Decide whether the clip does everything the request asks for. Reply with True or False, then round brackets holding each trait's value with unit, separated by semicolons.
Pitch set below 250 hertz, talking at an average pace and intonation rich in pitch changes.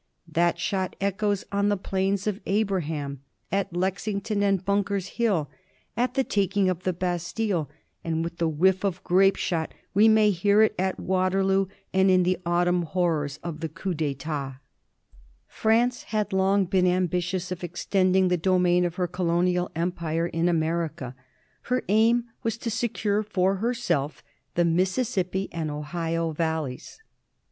False (185 Hz; 155 wpm; 2.9 semitones)